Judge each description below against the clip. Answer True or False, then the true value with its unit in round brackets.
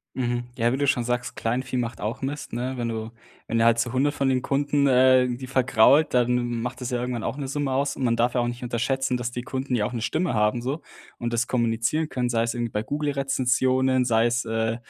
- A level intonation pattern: True (2.0 semitones)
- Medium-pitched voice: False (125 Hz)